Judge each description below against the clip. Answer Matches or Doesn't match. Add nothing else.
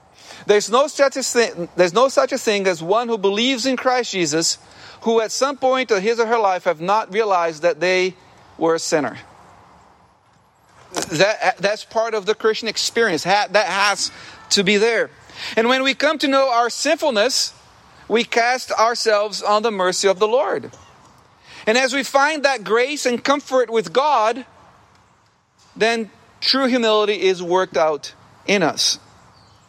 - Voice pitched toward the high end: Matches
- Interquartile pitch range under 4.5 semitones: Doesn't match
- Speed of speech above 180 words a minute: Doesn't match